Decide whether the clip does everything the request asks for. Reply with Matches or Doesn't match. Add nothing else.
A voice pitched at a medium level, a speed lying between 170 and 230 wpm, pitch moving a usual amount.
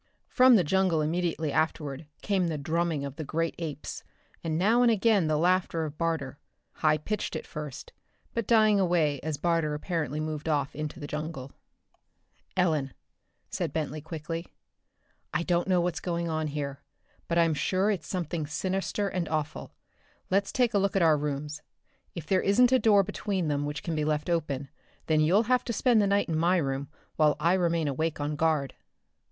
Matches